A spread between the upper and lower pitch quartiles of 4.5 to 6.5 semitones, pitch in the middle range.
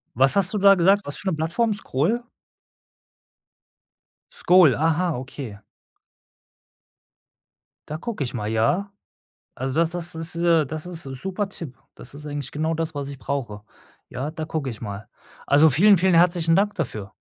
Yes: average, 4.8 semitones; medium, 160 Hz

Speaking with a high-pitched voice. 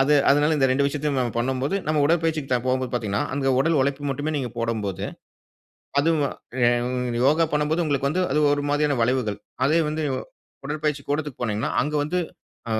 No: medium, 140 Hz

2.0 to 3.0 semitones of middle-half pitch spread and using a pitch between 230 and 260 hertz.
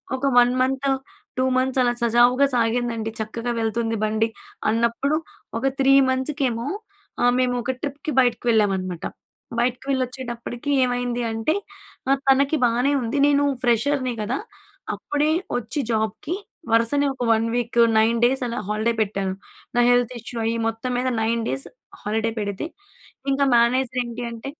Yes: narrow, 2.5 semitones; high, 240 Hz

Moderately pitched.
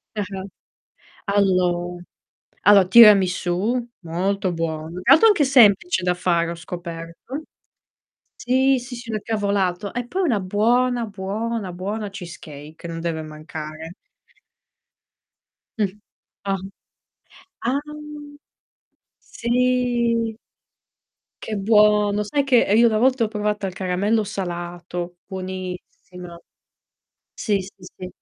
No: high, 200 Hz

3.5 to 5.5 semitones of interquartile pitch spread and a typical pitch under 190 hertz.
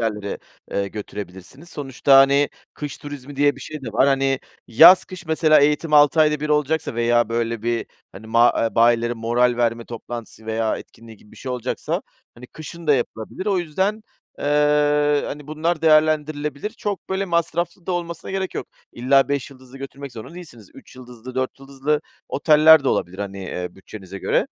Yes: average, 4.7 semitones; medium, 140 Hz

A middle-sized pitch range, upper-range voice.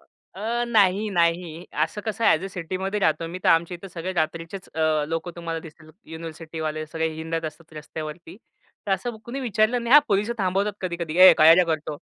No: average, 3.4 semitones; medium, 170 Hz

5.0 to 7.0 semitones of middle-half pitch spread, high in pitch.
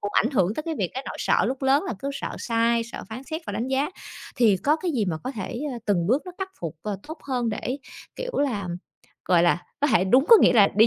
Yes: wide, 5.4 semitones; high, 240 Hz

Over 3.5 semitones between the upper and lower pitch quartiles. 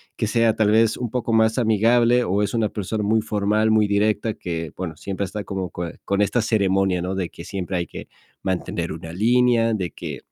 No: average, 2.9 semitones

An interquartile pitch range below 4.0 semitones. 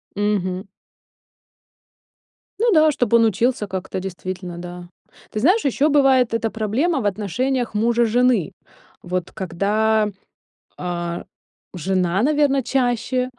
No: wide, 5.5 semitones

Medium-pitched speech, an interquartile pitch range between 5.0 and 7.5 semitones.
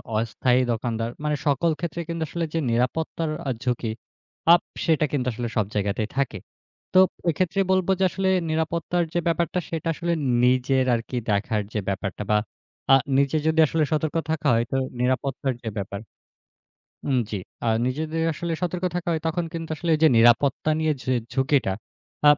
Yes: medium, 145 Hz; wide, 5.6 semitones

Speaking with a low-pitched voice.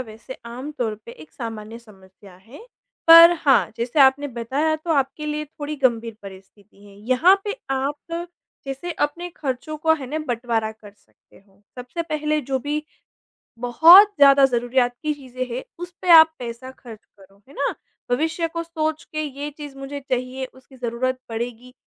No: very high, 265 Hz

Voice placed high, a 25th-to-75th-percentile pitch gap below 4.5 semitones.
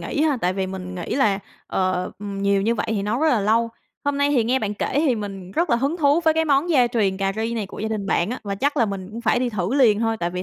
No: high, 220 Hz; average, 5.0 semitones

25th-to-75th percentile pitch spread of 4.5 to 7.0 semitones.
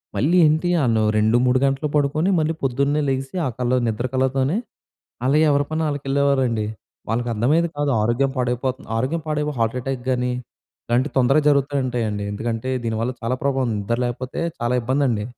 No: average, 3.0 semitones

